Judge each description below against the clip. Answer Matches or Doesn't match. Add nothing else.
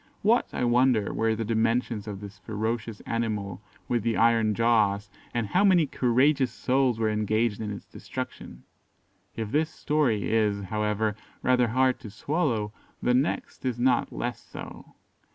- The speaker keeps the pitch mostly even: Doesn't match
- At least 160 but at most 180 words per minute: Doesn't match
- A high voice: Doesn't match